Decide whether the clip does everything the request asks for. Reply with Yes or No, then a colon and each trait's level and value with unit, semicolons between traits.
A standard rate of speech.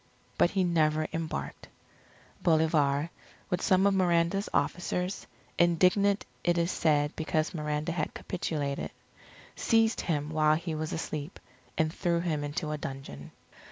No: slow, 130 wpm